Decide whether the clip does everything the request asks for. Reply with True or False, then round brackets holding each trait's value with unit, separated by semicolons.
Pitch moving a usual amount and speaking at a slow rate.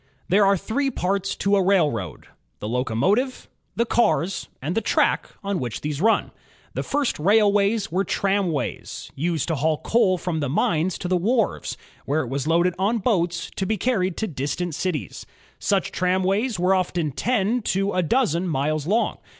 False (4.4 semitones; 175 wpm)